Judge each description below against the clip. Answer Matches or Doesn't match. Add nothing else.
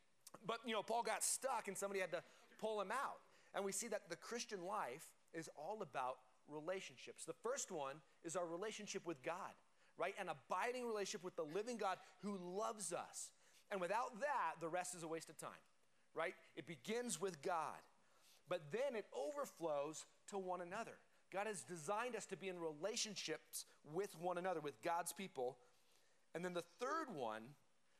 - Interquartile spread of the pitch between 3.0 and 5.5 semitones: Matches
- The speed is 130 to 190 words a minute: Matches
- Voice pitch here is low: Doesn't match